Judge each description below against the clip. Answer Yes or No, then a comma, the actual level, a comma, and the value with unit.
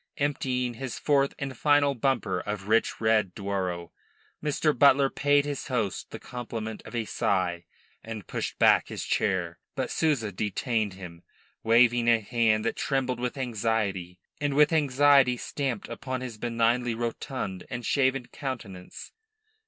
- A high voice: No, low, 120 Hz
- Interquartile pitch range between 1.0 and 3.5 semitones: No, average, 4.3 semitones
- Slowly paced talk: No, average, 145 wpm